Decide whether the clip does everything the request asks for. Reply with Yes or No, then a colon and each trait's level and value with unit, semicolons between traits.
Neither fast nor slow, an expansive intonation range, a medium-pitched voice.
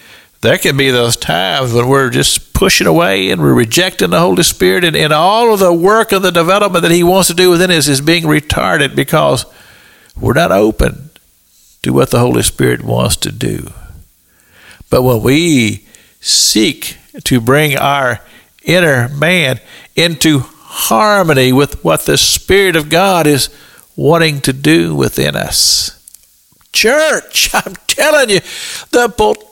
Yes: average, 155 wpm; wide, 6.3 semitones; medium, 155 Hz